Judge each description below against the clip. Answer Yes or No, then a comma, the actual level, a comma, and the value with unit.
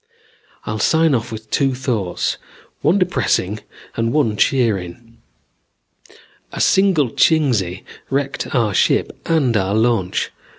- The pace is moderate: No, slow, 115 wpm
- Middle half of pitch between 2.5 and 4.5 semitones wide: No, average, 5.0 semitones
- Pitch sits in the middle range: No, low, 120 Hz